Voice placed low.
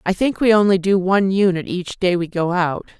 No: high, 190 Hz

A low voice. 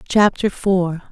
No: medium, 185 Hz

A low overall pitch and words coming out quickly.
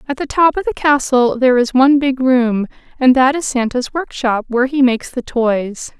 No: very high, 260 Hz; fast, 220 wpm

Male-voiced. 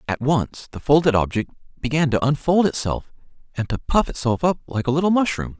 Yes: male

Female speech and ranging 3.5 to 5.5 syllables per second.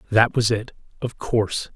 No: male; 4.8 syllables/s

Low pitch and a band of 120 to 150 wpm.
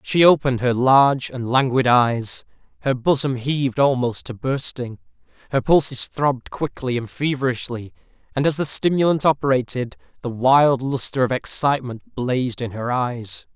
Yes: low, 130 Hz; average, 145 wpm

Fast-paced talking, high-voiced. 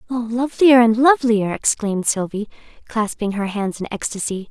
No: slow, 135 wpm; high, 225 Hz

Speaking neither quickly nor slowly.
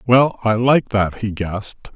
Yes: average, 185 wpm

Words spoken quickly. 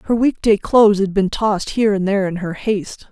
Yes: fast, 250 wpm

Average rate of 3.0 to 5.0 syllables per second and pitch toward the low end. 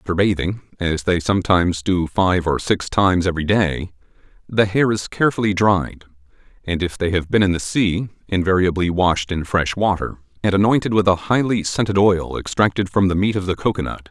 No: 5.4 syllables/s; very low, 95 Hz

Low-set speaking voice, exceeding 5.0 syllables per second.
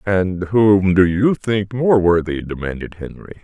No: very low, 95 Hz; 4.0 syllables/s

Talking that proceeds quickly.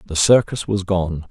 No: average, 185 wpm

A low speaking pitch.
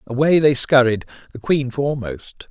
Yes: low, 130 Hz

